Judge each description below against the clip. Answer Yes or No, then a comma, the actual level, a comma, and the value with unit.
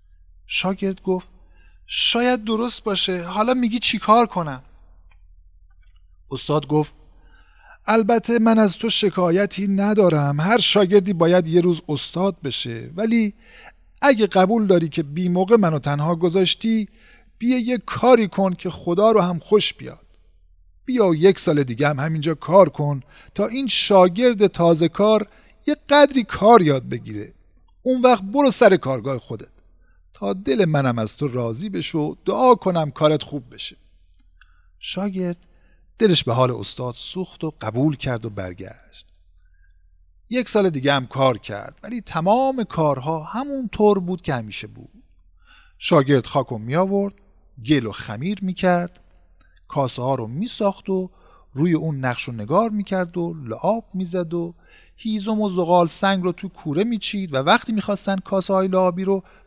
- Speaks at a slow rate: No, average, 150 wpm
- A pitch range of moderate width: No, wide, 7.9 semitones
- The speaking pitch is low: No, medium, 175 Hz